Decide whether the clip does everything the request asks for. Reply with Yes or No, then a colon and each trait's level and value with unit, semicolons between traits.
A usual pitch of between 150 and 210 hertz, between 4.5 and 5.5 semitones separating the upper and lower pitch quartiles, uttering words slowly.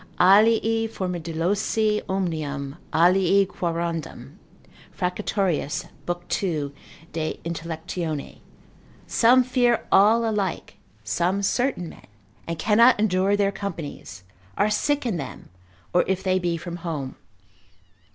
No: medium, 185 Hz; average, 4.1 semitones; slow, 105 wpm